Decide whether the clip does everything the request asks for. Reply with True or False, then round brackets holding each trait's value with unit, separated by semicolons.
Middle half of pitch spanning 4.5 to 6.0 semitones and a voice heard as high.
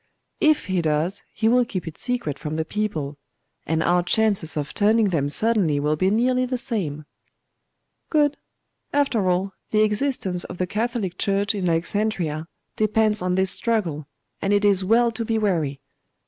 True (5.2 semitones; 200 Hz)